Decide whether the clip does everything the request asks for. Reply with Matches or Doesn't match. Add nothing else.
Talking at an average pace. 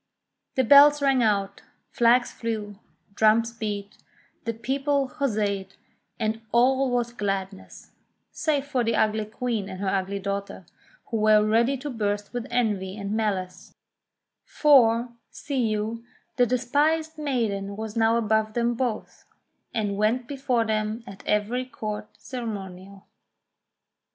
Doesn't match